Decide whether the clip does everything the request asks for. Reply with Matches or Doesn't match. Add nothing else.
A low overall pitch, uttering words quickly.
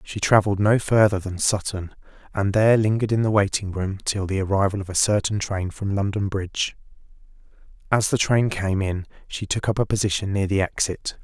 Doesn't match